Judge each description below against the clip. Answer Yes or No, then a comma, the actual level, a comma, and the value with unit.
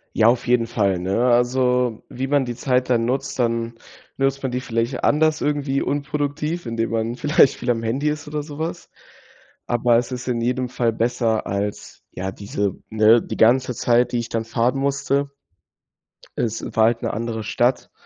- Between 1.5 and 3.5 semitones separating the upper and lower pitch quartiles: Yes, average, 2.9 semitones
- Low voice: Yes, low, 120 Hz